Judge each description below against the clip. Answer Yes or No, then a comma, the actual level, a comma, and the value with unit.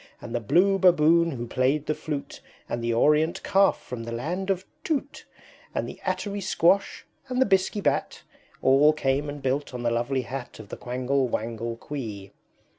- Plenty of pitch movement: Yes, wide, 7.1 semitones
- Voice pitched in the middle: Yes, medium, 145 Hz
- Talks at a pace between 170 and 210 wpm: Yes, average, 180 wpm